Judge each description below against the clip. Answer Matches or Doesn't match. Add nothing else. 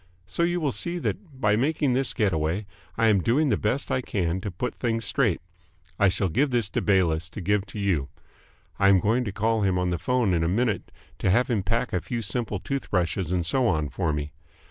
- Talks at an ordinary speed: Doesn't match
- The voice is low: Matches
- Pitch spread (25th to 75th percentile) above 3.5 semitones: Matches